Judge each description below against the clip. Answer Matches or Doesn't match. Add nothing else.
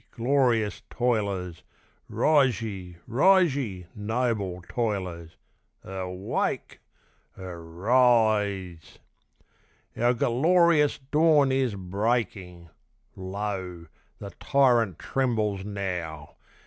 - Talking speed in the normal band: Doesn't match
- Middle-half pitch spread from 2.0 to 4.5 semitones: Doesn't match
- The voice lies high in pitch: Doesn't match